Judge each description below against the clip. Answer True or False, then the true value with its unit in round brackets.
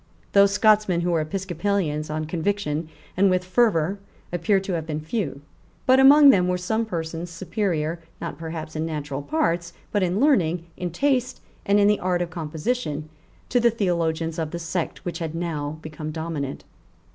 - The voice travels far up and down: False (4.1 semitones)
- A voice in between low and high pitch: True (170 Hz)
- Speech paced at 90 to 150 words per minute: False (170 wpm)